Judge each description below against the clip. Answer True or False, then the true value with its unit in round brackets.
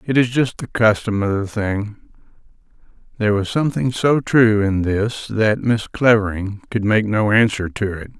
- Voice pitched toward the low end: True (110 Hz)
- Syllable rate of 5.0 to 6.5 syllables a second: False (4.7 syllables/s)